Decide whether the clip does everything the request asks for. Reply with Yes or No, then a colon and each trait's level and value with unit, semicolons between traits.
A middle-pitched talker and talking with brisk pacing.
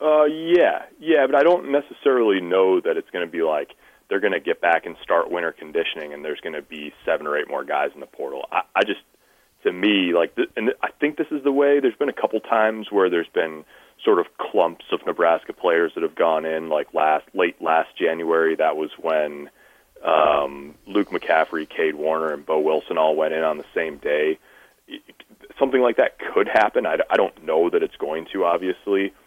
Yes: medium, 145 Hz; fast, 210 wpm